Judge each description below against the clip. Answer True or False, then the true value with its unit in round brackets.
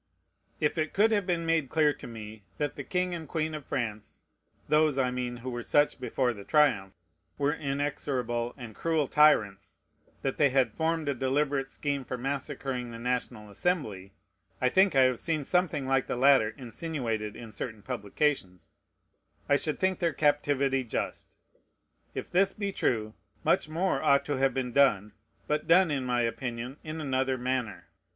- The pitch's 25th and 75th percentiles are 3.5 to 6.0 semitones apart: True (4.1 semitones)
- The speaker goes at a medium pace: True (170 wpm)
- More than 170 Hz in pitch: False (135 Hz)